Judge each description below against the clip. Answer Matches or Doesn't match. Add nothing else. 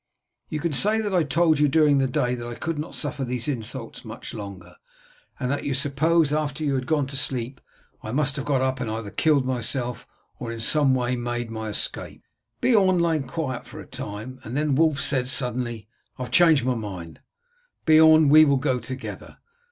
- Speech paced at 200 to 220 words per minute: Matches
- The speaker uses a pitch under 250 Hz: Matches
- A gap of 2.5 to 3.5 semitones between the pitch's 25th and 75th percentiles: Doesn't match